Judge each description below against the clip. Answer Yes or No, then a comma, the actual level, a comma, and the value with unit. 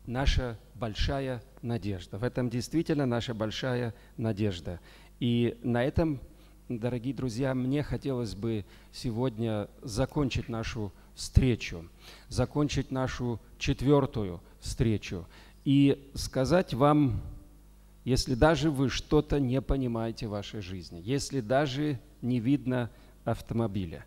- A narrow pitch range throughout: No, average, 3.8 semitones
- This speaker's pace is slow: Yes, slow, 105 wpm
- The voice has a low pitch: Yes, low, 125 Hz